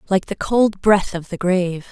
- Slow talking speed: No, fast, 220 wpm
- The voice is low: No, high, 190 Hz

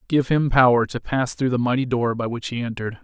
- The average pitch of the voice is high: No, low, 125 Hz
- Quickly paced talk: Yes, fast, 255 wpm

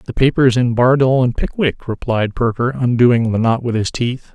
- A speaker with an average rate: Yes, average, 195 wpm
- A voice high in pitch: No, low, 120 Hz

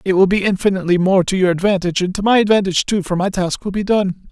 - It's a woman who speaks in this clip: No, male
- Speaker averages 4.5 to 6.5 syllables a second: No, 6.9 syllables/s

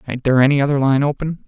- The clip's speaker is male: Yes, male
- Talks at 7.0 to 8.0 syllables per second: Yes, 7.6 syllables/s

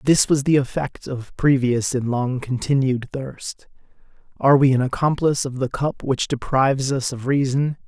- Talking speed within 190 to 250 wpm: No, average, 170 wpm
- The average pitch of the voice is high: No, low, 135 Hz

